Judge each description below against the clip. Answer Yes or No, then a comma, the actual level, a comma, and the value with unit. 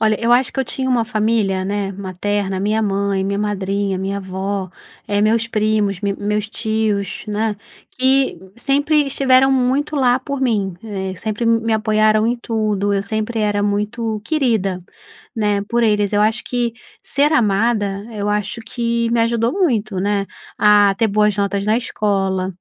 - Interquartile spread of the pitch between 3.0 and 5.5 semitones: No, narrow, 2.6 semitones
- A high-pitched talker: Yes, high, 215 Hz